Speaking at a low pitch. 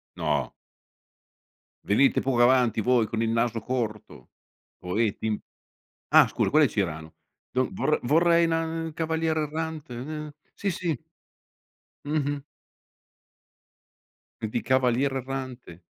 Yes: low, 130 Hz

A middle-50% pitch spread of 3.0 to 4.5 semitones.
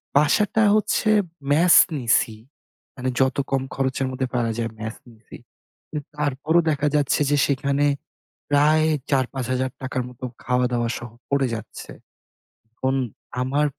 No: narrow, 2.6 semitones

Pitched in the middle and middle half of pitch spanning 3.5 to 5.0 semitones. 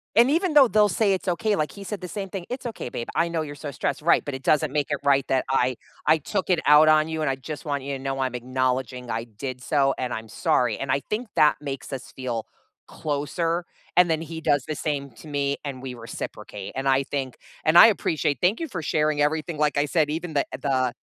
Yes: medium, 145 Hz; average, 4.1 semitones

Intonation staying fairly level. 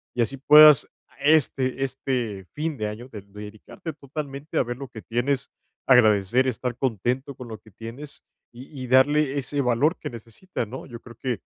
No: average, 3.3 semitones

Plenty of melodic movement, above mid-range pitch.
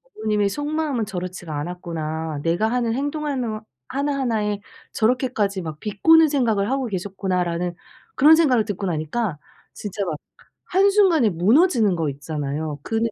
Yes: wide, 7.0 semitones; high, 210 Hz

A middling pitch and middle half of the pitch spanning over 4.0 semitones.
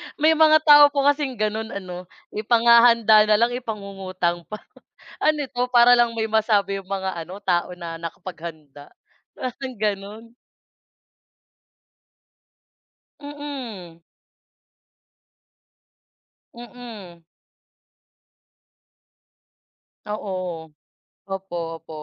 No: high, 215 Hz; average, 5.1 semitones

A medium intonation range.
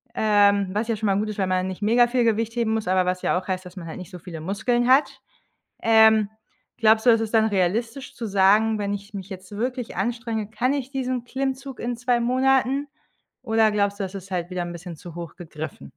Yes: average, 4.1 semitones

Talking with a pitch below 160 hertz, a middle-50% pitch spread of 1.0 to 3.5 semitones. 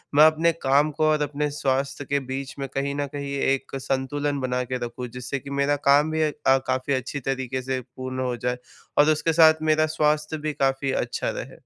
Yes: medium, 140 Hz; narrow, 2.4 semitones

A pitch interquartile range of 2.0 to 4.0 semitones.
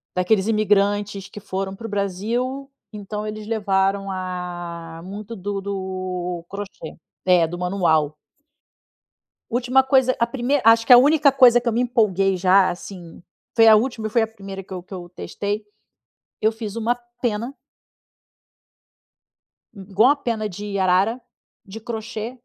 Yes: average, 3.4 semitones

